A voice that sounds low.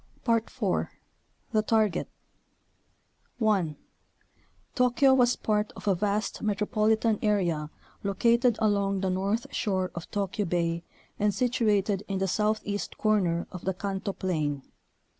No: high, 205 Hz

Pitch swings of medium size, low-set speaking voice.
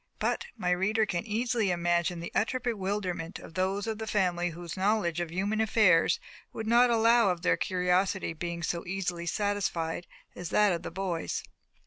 No: average, 3.7 semitones; medium, 185 Hz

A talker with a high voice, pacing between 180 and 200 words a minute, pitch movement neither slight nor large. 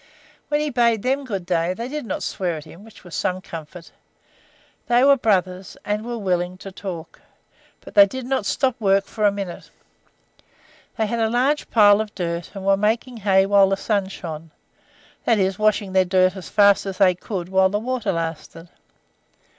Yes: high, 195 Hz; average, 190 wpm; average, 3.4 semitones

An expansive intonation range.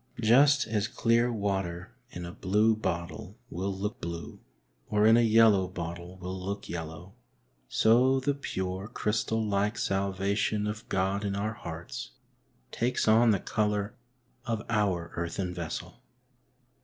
No: average, 3.3 semitones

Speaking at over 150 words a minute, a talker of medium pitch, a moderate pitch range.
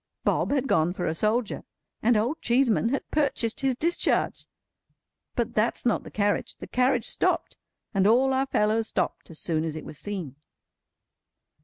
No: average, 165 wpm; high, 225 Hz; average, 4.8 semitones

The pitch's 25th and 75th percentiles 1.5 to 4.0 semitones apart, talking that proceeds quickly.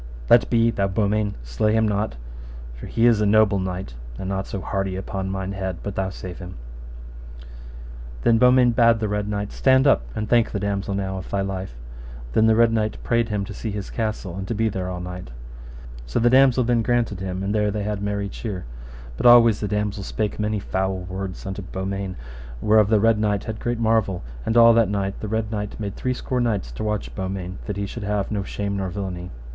Yes: narrow, 2.6 semitones; fast, 215 wpm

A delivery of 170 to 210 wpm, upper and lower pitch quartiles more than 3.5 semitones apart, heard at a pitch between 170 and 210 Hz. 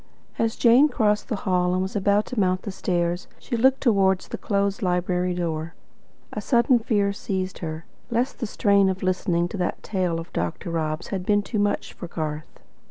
No: average, 190 wpm; average, 2.9 semitones; high, 190 Hz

